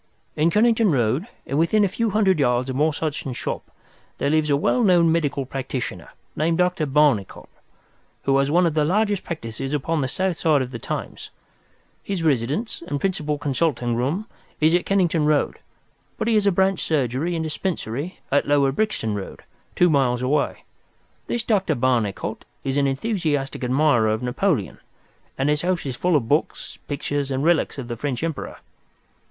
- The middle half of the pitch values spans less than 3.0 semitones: No, average, 4.9 semitones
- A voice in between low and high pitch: Yes, medium, 150 Hz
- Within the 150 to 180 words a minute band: Yes, average, 175 wpm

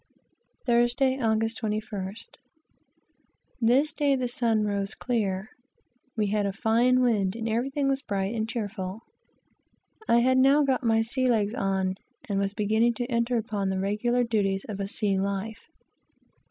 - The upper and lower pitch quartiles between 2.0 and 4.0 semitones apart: Yes, average, 3.3 semitones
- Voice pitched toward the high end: Yes, high, 225 Hz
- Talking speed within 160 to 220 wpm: No, average, 150 wpm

